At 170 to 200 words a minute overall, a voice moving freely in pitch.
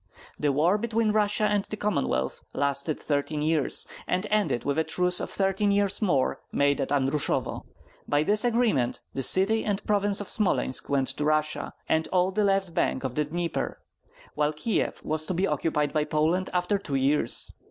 Yes: average, 180 wpm; wide, 5.7 semitones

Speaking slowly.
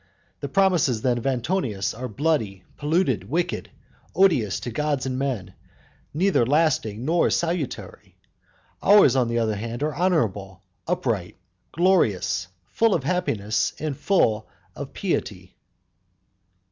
Yes: slow, 120 wpm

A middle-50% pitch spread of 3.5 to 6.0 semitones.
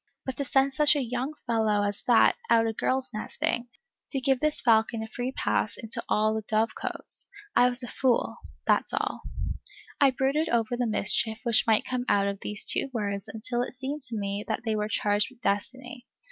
No: average, 3.1 semitones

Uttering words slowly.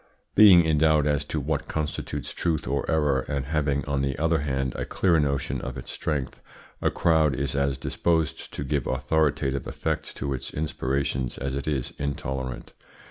No: average, 175 wpm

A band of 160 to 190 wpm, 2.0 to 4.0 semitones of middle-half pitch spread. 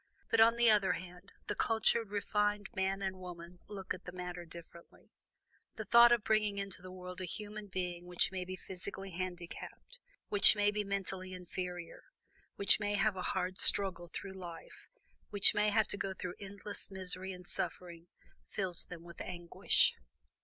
Yes: average, 170 wpm; narrow, 2.4 semitones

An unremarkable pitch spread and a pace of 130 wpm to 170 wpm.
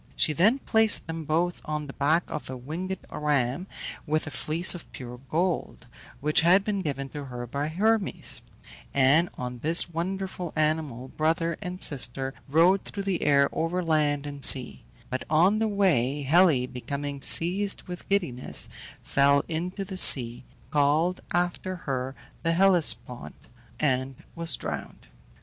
Yes: average, 4.4 semitones; average, 150 wpm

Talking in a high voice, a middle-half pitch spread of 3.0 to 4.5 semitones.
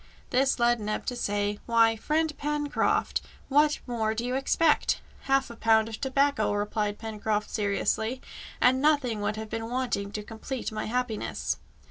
Yes: high, 230 Hz; average, 3.7 semitones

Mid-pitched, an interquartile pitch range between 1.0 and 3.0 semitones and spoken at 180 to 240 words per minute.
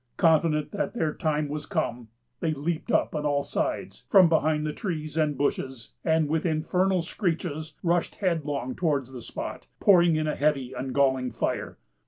No: medium, 155 Hz; average, 2.7 semitones; average, 170 wpm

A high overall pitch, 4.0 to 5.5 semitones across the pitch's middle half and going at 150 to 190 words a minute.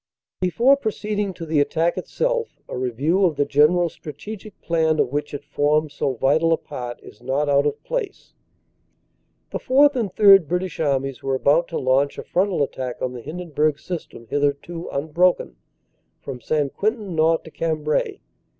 No: medium, 155 Hz; average, 4.4 semitones; average, 170 wpm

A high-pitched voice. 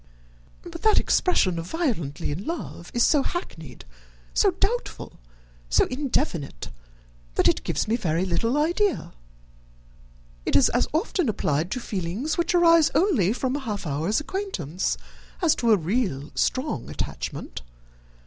Yes: high, 235 Hz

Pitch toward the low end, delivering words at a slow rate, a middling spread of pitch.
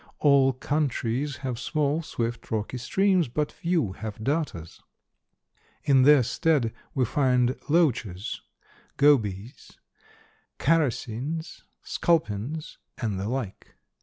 Yes: low, 130 Hz; slow, 100 wpm; average, 4.8 semitones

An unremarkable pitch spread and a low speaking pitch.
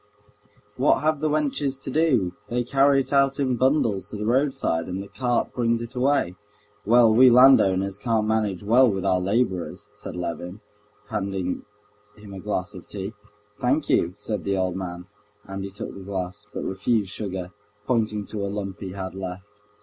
Yes: average, 4.9 semitones; low, 105 Hz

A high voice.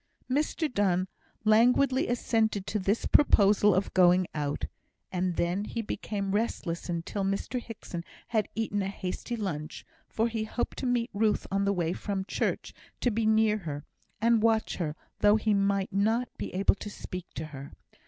Yes: high, 205 Hz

